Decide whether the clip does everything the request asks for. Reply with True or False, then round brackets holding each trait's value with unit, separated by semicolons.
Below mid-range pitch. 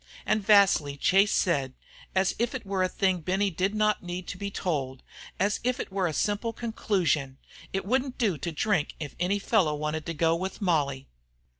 False (185 Hz)